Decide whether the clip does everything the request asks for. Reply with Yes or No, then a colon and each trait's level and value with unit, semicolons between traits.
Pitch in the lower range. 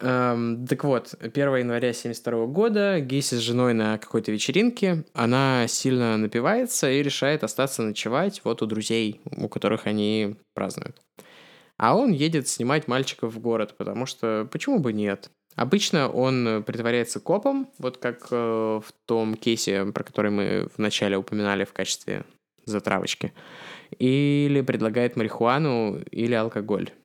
Yes: low, 120 Hz